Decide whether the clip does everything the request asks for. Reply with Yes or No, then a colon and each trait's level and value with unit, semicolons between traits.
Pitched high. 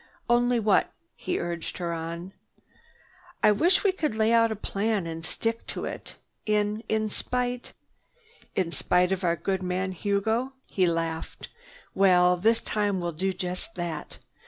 Yes: high, 195 Hz